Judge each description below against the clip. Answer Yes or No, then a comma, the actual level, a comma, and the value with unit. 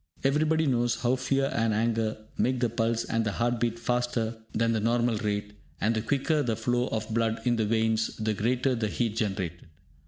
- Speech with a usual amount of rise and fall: No, narrow, 1.8 semitones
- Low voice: Yes, low, 115 Hz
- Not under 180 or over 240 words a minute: Yes, average, 195 wpm